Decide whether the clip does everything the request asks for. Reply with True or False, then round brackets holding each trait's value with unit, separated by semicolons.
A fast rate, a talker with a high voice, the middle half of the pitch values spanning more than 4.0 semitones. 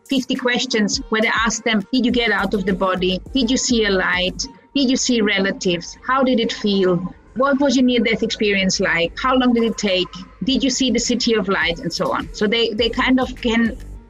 True (230 wpm; 230 Hz; 4.4 semitones)